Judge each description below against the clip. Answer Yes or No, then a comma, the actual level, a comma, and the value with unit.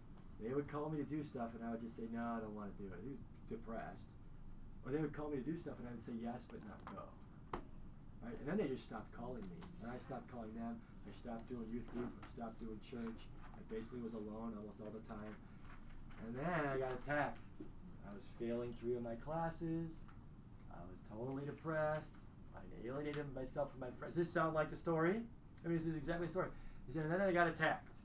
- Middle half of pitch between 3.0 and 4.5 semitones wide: No, average, 5.0 semitones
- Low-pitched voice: Yes, low, 125 Hz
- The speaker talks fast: Yes, fast, 230 wpm